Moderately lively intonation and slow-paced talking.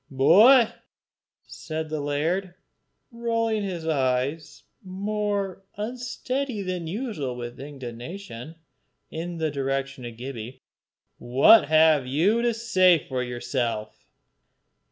No: wide, 7.3 semitones; slow, 100 wpm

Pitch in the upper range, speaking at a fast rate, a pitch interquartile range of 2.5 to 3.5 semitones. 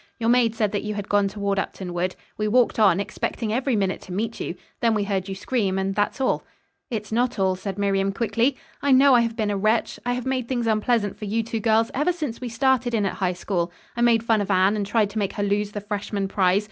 Yes: high, 210 Hz; fast, 255 wpm; average, 2.9 semitones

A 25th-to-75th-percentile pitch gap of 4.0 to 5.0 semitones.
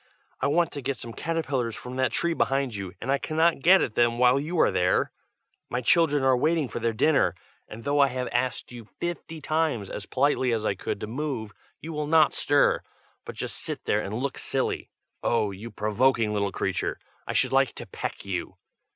Yes: average, 4.7 semitones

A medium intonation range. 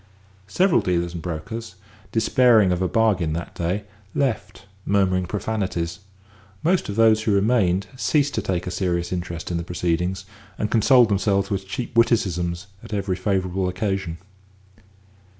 Yes: average, 3.8 semitones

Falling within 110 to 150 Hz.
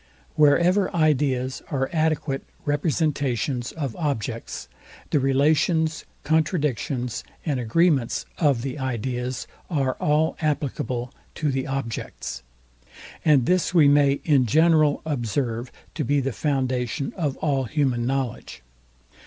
Yes: medium, 140 Hz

